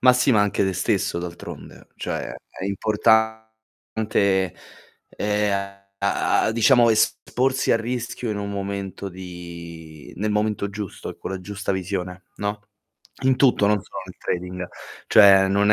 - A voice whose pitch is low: Yes, low, 100 Hz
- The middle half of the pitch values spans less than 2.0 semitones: No, average, 2.7 semitones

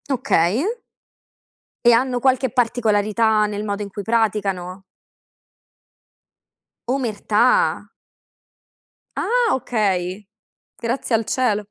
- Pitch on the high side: Yes, high, 220 Hz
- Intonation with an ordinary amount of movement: Yes, average, 3.4 semitones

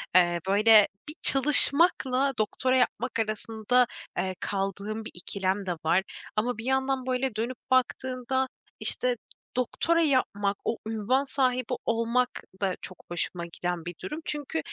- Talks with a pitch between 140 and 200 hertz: No, high, 230 Hz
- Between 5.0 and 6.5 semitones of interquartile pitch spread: No, average, 4.5 semitones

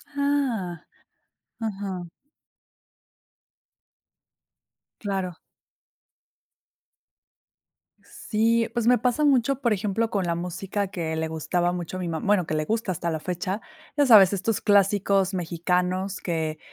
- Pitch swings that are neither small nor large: Yes, average, 4.1 semitones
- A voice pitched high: Yes, high, 195 Hz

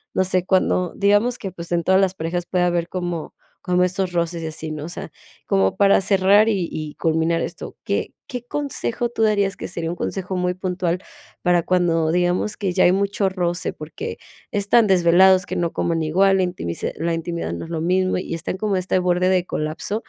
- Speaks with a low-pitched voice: No, medium, 180 Hz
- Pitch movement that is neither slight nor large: No, narrow, 2.3 semitones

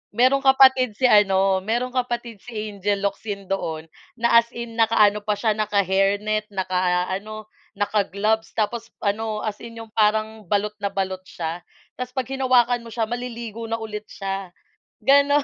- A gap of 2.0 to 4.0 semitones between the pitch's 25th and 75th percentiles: Yes, average, 2.9 semitones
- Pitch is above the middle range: Yes, high, 215 Hz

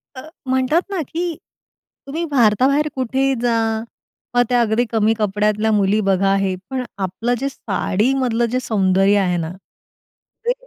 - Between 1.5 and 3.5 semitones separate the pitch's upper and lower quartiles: No, average, 4.7 semitones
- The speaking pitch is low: No, high, 230 Hz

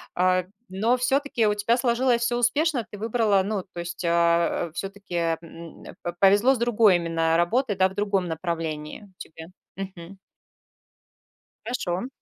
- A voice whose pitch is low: No, high, 195 Hz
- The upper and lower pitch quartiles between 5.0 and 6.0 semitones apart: Yes, wide, 5.4 semitones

